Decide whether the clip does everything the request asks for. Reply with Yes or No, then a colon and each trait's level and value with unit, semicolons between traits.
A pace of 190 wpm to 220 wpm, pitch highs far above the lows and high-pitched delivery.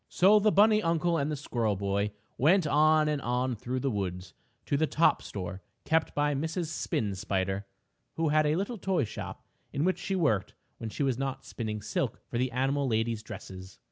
No: average, 195 wpm; wide, 6.9 semitones; low, 135 Hz